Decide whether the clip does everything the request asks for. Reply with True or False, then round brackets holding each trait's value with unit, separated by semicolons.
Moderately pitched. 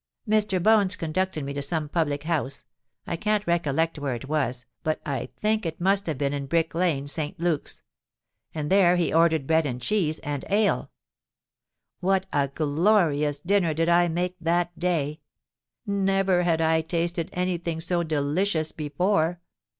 True (165 Hz)